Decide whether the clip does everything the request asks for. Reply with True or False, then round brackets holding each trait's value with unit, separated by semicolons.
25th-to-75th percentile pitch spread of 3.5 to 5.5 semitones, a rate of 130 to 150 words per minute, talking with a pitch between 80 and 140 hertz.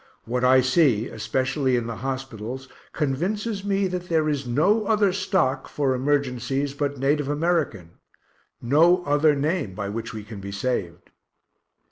True (5.2 semitones; 145 wpm; 135 Hz)